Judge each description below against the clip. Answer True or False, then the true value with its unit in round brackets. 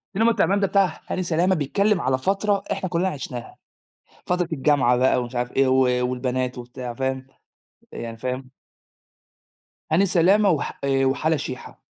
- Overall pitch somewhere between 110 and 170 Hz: True (140 Hz)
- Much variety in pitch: True (6.3 semitones)